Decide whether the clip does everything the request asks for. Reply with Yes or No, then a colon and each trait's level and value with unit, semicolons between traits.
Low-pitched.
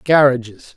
Yes: low, 130 Hz